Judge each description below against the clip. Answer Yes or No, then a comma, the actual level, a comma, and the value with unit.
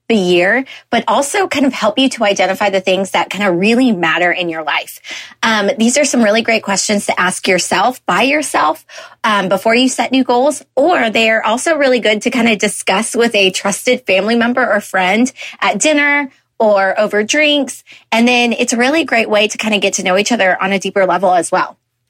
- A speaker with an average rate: No, fast, 220 wpm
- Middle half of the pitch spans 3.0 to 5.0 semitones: Yes, average, 4.3 semitones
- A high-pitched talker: Yes, high, 220 Hz